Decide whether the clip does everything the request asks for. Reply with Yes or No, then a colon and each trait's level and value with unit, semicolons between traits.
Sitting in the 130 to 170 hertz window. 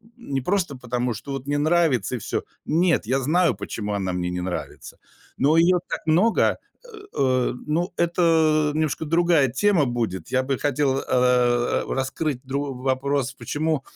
Yes: medium, 140 Hz